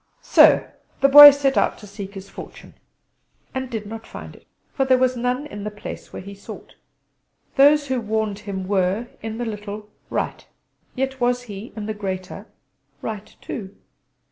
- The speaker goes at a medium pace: Yes, average, 170 wpm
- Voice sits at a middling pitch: No, high, 220 Hz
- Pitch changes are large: No, average, 4.1 semitones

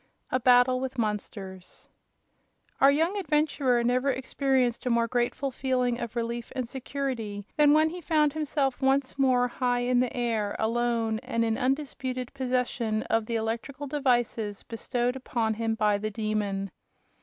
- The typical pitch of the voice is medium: No, high, 245 Hz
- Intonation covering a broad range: No, average, 2.9 semitones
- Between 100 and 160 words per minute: Yes, average, 150 wpm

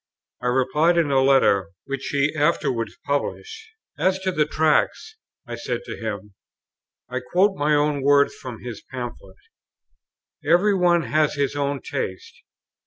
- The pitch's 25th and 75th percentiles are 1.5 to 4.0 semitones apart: No, average, 4.7 semitones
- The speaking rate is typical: Yes, average, 145 wpm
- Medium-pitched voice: Yes, medium, 145 Hz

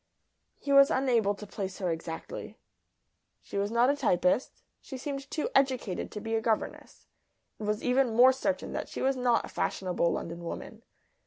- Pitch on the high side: Yes, high, 230 Hz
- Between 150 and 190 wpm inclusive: Yes, average, 175 wpm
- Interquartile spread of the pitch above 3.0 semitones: Yes, average, 4.9 semitones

